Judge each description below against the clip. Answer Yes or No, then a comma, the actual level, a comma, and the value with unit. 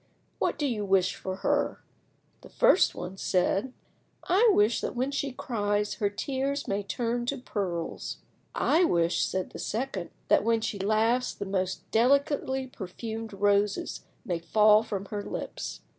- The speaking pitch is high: Yes, high, 215 Hz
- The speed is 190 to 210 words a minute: No, average, 155 wpm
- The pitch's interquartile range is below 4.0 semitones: No, average, 4.3 semitones